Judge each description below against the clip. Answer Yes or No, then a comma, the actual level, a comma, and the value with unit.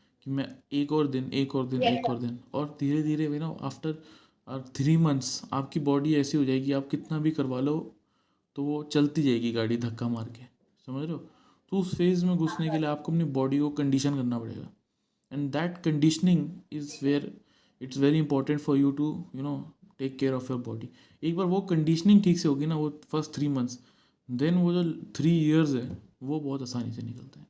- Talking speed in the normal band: No, fast, 205 wpm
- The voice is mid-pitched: Yes, medium, 145 Hz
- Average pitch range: Yes, average, 3.1 semitones